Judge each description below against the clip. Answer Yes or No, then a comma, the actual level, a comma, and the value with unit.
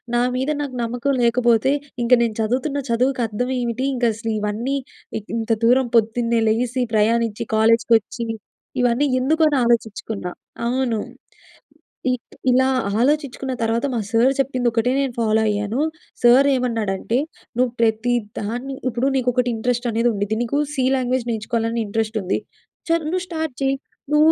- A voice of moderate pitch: No, high, 240 Hz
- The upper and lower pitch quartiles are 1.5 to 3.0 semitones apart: Yes, narrow, 2.5 semitones